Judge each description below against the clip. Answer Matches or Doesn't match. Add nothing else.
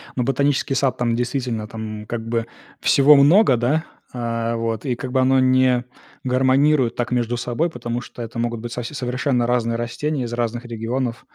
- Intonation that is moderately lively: Doesn't match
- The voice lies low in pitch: Matches